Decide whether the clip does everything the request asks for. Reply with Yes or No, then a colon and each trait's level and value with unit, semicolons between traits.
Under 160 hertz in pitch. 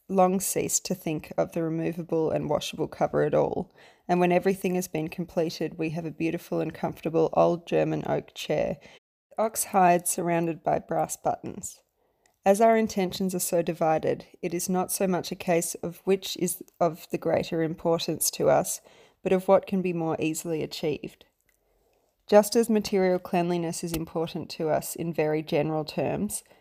No: medium, 170 Hz